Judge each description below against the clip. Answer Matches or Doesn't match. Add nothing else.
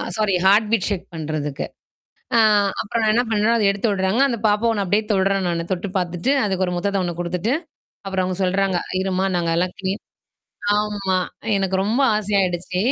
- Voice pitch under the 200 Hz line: Matches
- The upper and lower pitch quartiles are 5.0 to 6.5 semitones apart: Doesn't match